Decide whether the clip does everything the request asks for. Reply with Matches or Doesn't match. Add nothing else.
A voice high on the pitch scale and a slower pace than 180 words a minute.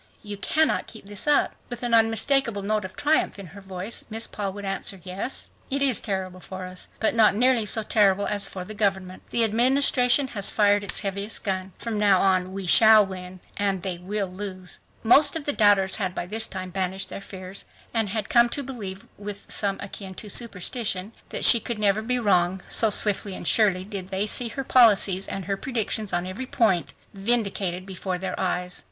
Doesn't match